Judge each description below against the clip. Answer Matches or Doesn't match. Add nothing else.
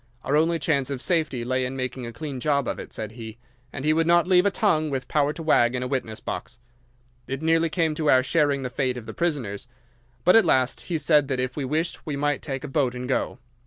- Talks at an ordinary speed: Doesn't match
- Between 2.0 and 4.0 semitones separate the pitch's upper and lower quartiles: Matches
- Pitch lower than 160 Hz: Matches